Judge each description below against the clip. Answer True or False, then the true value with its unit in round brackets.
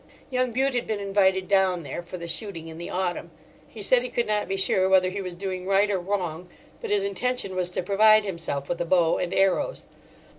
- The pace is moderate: False (225 wpm)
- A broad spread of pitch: False (3.0 semitones)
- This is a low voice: False (190 Hz)